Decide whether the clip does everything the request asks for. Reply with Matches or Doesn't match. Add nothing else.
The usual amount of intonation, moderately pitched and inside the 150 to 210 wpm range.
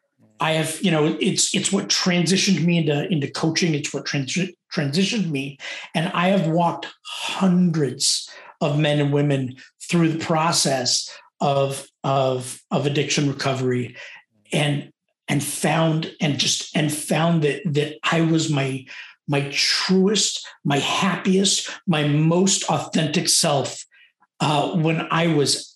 Doesn't match